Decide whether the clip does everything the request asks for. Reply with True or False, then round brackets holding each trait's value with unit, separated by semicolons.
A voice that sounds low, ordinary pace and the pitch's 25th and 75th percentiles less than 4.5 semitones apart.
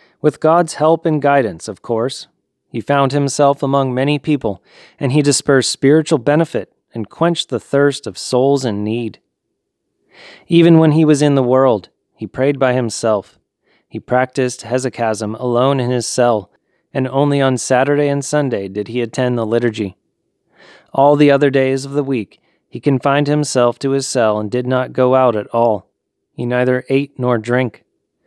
True (130 Hz; 170 wpm; 3.1 semitones)